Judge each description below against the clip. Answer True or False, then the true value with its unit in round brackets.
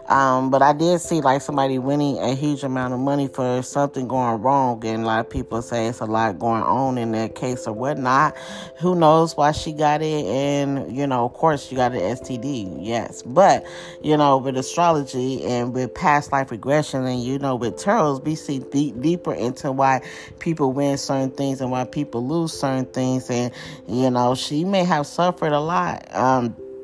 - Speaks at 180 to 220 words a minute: True (200 wpm)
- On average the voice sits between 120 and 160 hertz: True (135 Hz)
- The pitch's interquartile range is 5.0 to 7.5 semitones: False (2.5 semitones)